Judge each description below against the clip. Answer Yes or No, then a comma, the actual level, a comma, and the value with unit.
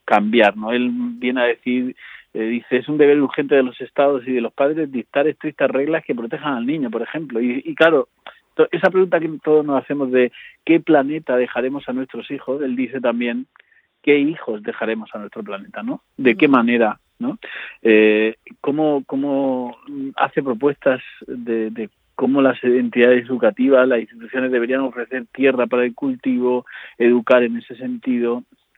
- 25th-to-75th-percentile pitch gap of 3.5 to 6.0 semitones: No, average, 3.1 semitones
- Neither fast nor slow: Yes, average, 170 wpm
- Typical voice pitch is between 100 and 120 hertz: No, low, 130 Hz